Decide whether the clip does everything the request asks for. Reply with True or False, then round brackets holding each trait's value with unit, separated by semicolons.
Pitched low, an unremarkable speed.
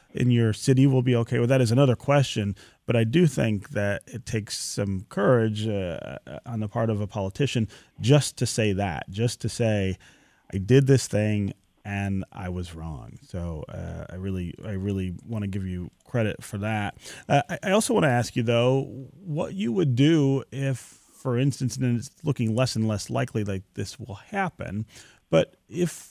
True (115 Hz; 195 wpm)